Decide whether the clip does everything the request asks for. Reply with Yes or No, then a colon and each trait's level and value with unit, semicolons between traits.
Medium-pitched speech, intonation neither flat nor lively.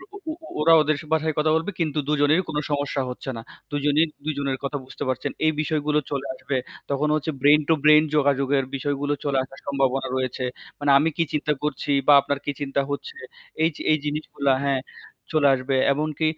No: medium, 145 Hz; narrow, 1.8 semitones